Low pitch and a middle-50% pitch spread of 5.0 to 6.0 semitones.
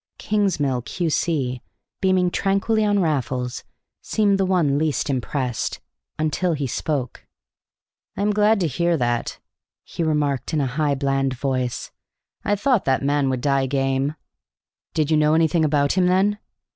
No: medium, 150 Hz; average, 5.3 semitones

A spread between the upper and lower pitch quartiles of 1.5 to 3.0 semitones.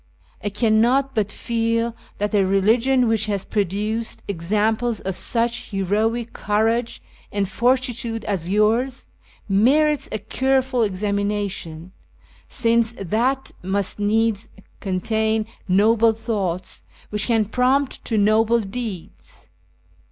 Yes: narrow, 2.6 semitones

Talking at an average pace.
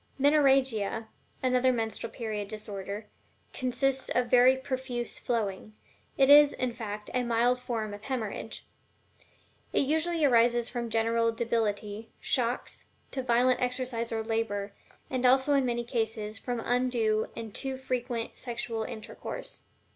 No: slow, 130 wpm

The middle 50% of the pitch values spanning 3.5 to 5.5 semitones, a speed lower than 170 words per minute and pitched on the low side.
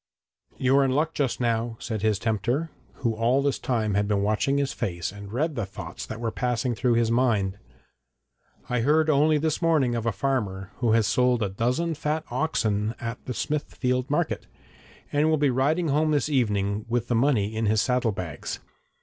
No: average, 4.6 semitones; average, 190 wpm; low, 120 Hz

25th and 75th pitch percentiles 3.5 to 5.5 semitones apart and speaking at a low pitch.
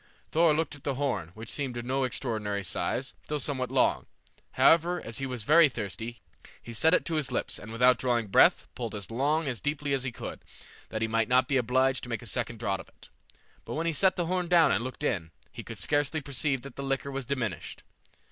Yes: average, 4.1 semitones; low, 130 Hz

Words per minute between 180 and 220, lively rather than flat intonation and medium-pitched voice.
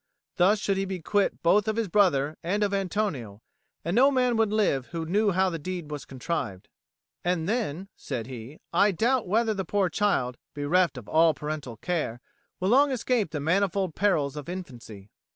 Yes: average, 185 wpm; wide, 5.8 semitones; medium, 180 Hz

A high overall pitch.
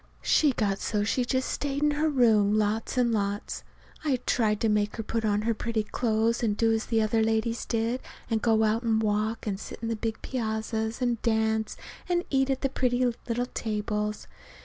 Yes: high, 225 Hz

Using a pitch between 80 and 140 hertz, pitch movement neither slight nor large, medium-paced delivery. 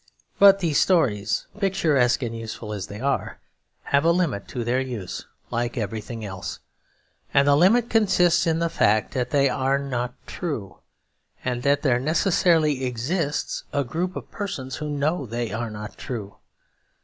No: low, 135 Hz; wide, 5.8 semitones; average, 160 wpm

